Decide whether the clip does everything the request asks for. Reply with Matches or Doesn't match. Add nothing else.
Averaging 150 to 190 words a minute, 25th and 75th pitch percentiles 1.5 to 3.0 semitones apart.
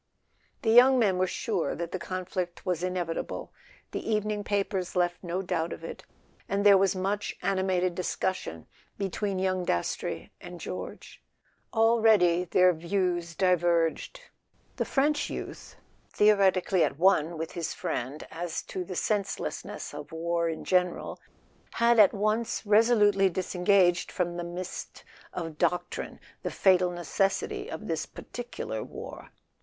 Doesn't match